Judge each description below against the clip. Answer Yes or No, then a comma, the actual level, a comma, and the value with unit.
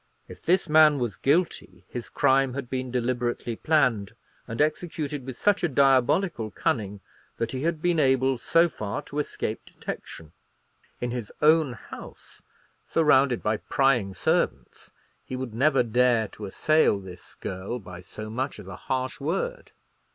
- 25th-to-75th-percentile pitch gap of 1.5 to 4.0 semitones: No, average, 4.9 semitones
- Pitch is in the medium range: No, low, 130 Hz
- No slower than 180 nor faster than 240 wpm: No, average, 150 wpm